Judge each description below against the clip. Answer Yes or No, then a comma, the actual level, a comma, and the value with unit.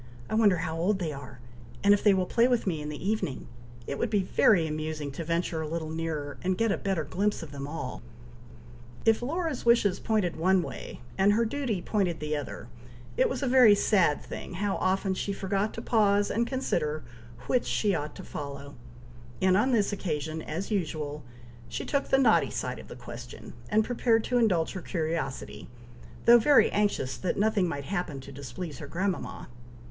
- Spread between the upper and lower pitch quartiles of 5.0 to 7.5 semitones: Yes, wide, 5.6 semitones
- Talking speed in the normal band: Yes, average, 195 wpm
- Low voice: No, medium, 185 Hz